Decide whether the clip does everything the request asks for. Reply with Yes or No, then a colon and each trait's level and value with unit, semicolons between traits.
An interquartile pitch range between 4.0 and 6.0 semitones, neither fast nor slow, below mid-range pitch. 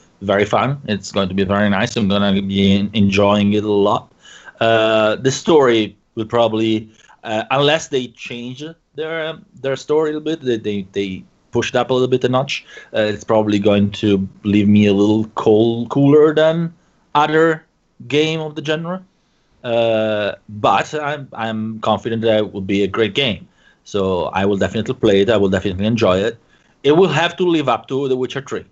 Yes: average, 5.2 semitones; average, 195 wpm; low, 110 Hz